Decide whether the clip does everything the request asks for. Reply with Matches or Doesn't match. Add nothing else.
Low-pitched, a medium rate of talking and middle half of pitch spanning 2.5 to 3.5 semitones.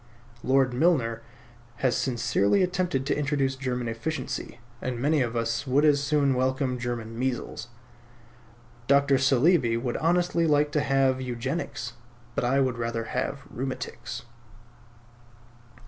Doesn't match